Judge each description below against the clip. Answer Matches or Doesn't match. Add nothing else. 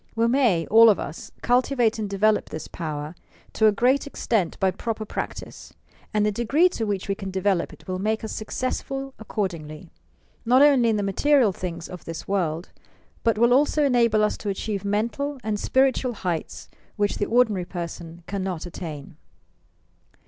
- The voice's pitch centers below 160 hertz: Doesn't match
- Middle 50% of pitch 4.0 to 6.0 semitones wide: Matches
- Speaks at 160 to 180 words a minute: Matches